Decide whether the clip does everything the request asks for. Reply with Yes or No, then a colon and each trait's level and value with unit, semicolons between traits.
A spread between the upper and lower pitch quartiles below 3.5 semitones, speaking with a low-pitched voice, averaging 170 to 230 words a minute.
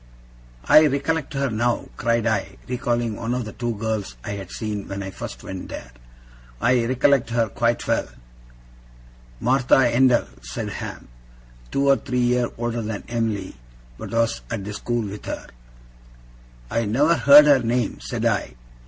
No: average, 2.9 semitones; low, 115 Hz; average, 160 wpm